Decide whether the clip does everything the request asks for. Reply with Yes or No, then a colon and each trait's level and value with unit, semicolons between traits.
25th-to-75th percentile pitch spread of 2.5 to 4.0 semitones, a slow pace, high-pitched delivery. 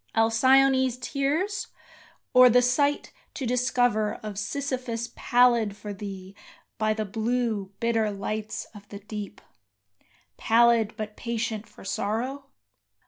Yes: average, 2.9 semitones; slow, 115 wpm; high, 230 Hz